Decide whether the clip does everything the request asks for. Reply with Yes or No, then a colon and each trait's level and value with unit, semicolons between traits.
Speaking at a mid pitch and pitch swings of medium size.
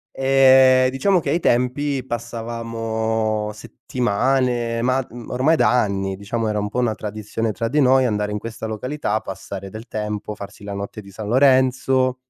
No: low, 115 Hz; average, 3.5 semitones